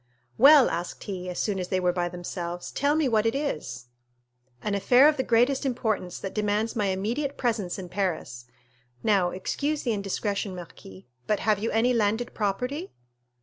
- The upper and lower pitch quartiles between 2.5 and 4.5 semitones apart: No, average, 5.2 semitones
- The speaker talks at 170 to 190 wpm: Yes, average, 175 wpm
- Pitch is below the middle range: No, high, 210 Hz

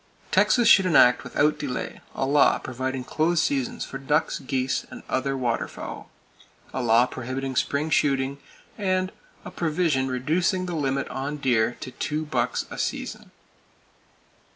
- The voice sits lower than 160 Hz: Yes, low, 135 Hz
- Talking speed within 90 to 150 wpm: Yes, average, 140 wpm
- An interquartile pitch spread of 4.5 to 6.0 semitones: No, average, 3.6 semitones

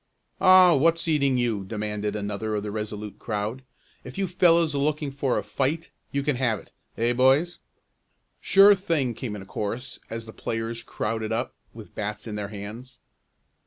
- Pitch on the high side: No, low, 120 Hz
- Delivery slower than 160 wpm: No, average, 175 wpm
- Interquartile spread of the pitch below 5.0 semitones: No, average, 5.3 semitones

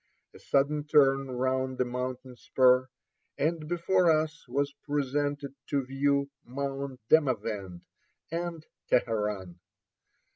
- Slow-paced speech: Yes, slow, 115 wpm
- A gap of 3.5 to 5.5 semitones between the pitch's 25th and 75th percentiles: No, narrow, 2.6 semitones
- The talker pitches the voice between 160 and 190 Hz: No, low, 135 Hz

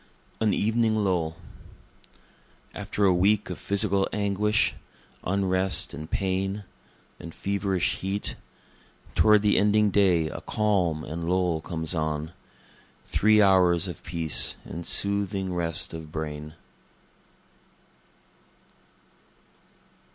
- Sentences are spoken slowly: Yes, slow, 100 wpm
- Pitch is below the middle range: Yes, very low, 95 Hz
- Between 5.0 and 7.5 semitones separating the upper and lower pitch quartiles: No, average, 3.5 semitones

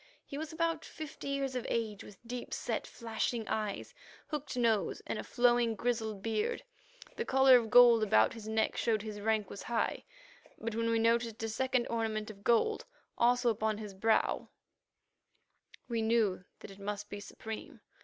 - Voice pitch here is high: Yes, high, 225 Hz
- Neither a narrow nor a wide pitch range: No, narrow, 2.2 semitones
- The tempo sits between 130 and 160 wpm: No, average, 175 wpm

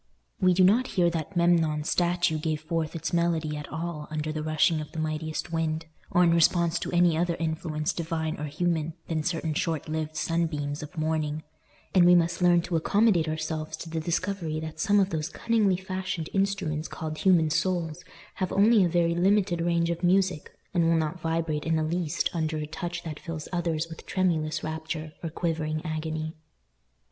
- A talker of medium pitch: Yes, medium, 165 Hz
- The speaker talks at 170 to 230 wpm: Yes, average, 185 wpm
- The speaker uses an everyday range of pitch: No, narrow, 1.9 semitones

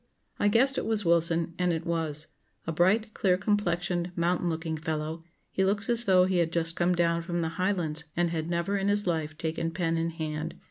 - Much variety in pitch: No, narrow, 2.4 semitones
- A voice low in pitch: No, medium, 170 Hz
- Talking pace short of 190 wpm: No, fast, 205 wpm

